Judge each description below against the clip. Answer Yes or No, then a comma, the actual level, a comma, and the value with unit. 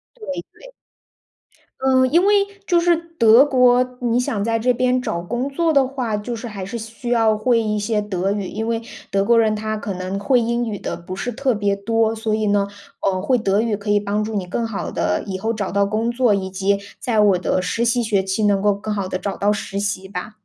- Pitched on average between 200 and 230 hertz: Yes, high, 215 Hz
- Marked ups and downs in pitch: No, average, 3.1 semitones